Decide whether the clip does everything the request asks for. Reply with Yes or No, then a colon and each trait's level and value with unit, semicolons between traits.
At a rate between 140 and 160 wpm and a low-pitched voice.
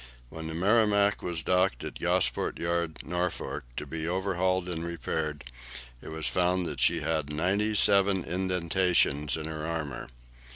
Yes: average, 150 wpm; very low, 85 Hz